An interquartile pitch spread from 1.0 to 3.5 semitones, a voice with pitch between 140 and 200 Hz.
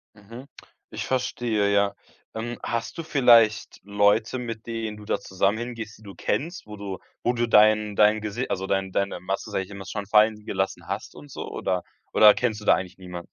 No: narrow, 2.6 semitones; low, 105 Hz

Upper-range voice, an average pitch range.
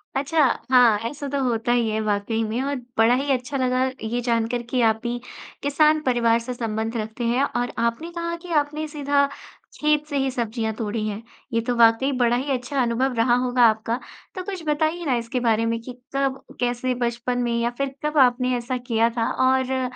Yes: high, 245 Hz; average, 3.0 semitones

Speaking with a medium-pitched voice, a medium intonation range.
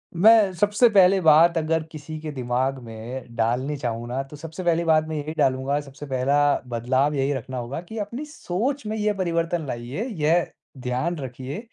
Yes: medium, 150 Hz; average, 5.0 semitones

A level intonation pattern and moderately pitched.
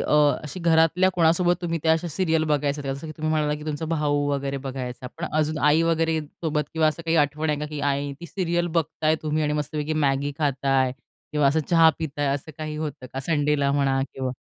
Yes: narrow, 2.2 semitones; medium, 150 Hz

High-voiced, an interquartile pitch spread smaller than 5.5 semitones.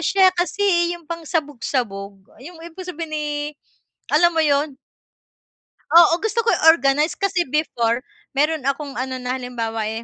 Yes: very high, 300 Hz; average, 5.1 semitones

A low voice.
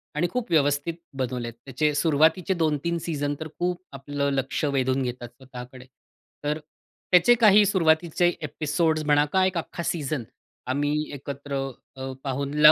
No: medium, 150 Hz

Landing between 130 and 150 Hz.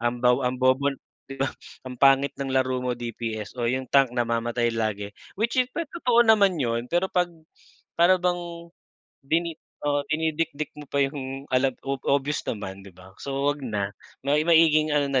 Yes: low, 135 Hz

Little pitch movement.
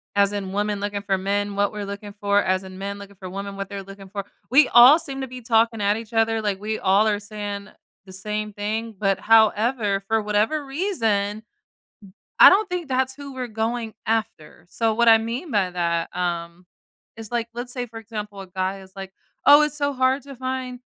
No: average, 3.2 semitones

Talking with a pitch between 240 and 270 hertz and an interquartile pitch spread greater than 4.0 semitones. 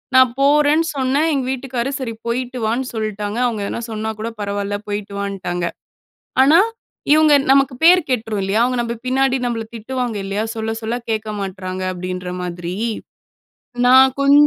No: high, 230 Hz; average, 4.4 semitones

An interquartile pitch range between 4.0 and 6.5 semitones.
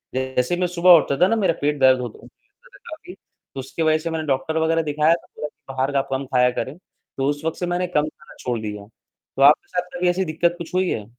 Yes: average, 4.5 semitones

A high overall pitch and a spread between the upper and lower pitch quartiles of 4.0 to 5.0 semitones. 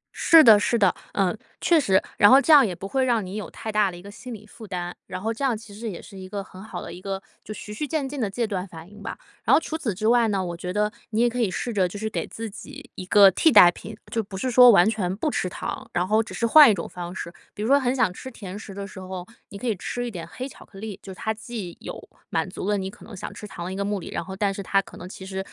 No: high, 205 Hz; average, 3.3 semitones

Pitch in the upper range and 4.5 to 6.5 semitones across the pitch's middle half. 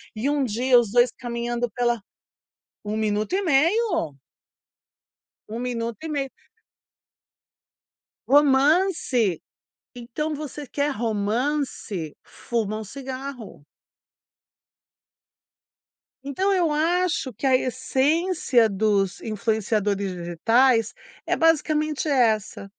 Yes: high, 245 Hz; average, 5.2 semitones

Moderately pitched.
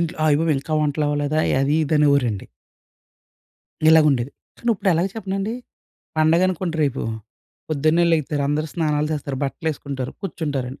Yes: medium, 155 Hz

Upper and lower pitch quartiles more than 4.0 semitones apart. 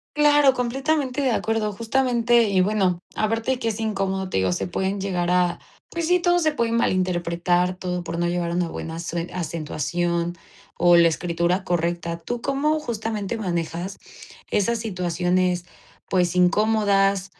Yes: average, 4.7 semitones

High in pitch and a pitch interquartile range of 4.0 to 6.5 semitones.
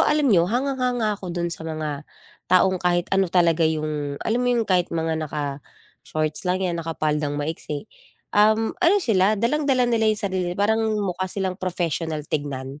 No: medium, 180 Hz; wide, 5.6 semitones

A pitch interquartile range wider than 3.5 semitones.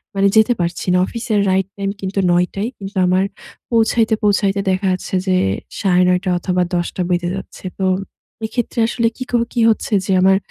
No: average, 3.1 semitones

